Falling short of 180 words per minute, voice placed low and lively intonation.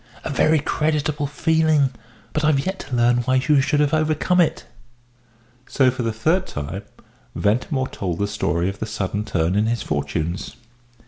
Yes: average, 170 wpm; low, 130 Hz; wide, 6.9 semitones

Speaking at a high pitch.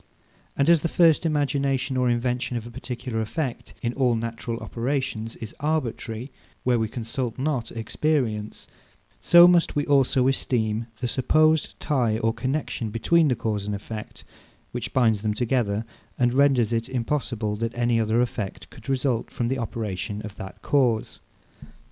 No: low, 120 Hz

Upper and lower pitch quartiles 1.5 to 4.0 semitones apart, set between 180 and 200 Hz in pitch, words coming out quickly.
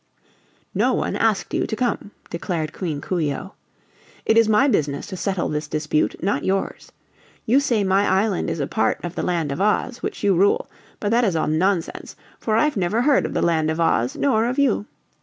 No: wide, 5.4 semitones; high, 190 Hz; fast, 210 wpm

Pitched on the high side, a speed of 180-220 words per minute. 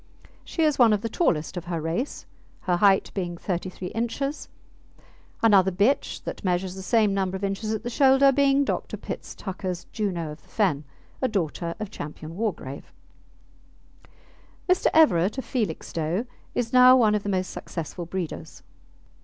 No: high, 195 Hz; average, 160 wpm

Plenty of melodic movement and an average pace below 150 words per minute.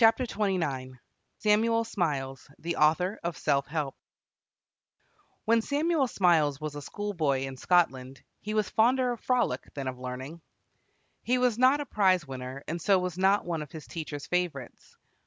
No: wide, 7.4 semitones; average, 155 wpm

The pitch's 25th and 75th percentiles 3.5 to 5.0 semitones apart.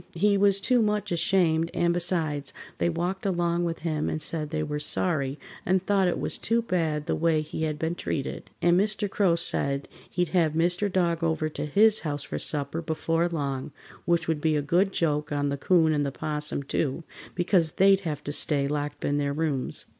No: average, 3.1 semitones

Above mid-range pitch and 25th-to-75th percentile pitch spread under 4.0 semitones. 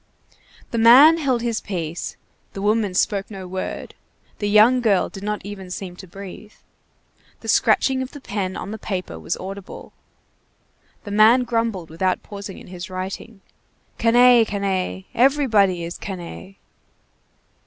Yes: high, 200 Hz; average, 3.5 semitones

